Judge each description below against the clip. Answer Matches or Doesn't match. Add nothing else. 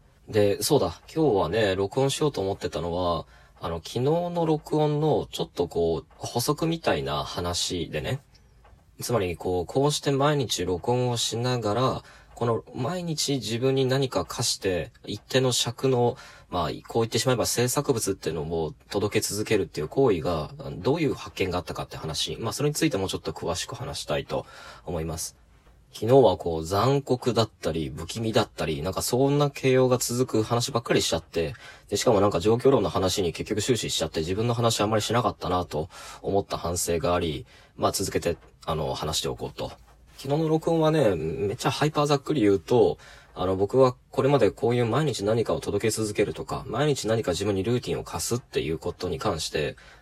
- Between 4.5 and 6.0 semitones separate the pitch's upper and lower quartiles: Doesn't match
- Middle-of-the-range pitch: Doesn't match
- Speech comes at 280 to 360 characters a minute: Doesn't match